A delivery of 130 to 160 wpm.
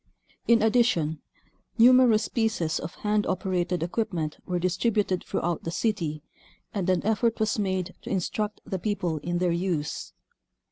Yes: average, 140 wpm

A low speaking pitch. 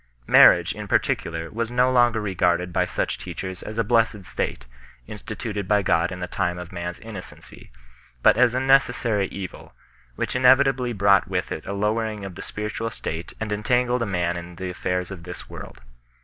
Yes: low, 100 Hz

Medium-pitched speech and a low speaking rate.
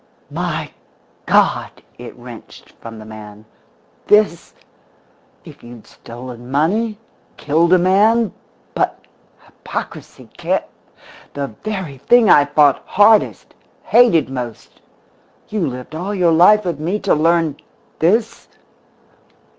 Yes: medium, 165 Hz; slow, 110 wpm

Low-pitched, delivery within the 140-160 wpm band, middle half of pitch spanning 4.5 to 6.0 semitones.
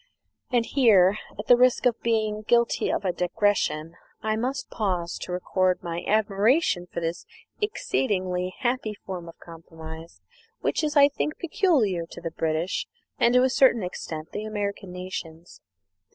No: high, 200 Hz; average, 150 wpm; wide, 5.4 semitones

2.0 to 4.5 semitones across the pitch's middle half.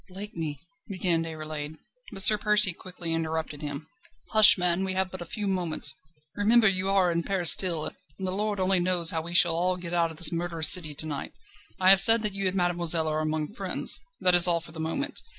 Yes: average, 2.9 semitones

